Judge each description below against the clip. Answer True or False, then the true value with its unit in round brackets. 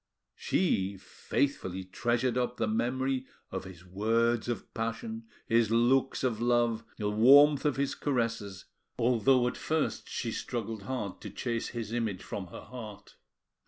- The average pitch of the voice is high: False (115 Hz)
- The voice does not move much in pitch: False (3.2 semitones)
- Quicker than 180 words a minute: False (145 wpm)